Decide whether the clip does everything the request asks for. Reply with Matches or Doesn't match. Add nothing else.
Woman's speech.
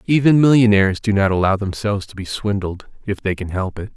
Doesn't match